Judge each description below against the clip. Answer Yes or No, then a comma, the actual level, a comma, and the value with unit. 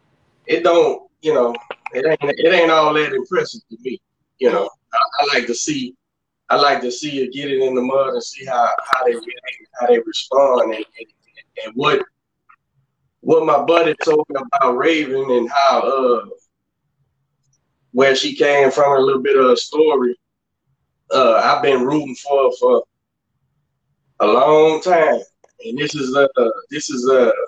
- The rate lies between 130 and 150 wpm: No, average, 170 wpm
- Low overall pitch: No, medium, 155 Hz